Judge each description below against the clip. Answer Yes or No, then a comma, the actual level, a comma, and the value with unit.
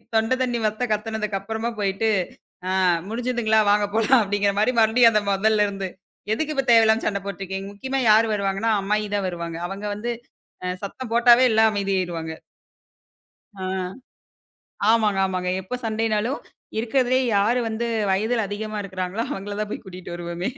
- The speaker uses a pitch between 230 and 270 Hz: No, high, 215 Hz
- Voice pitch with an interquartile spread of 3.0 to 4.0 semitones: No, narrow, 2.6 semitones